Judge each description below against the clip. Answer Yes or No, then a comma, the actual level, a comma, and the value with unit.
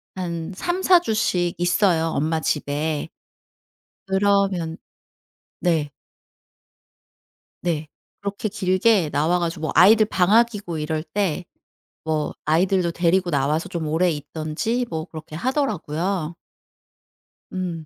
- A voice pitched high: No, medium, 175 Hz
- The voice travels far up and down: No, average, 3.7 semitones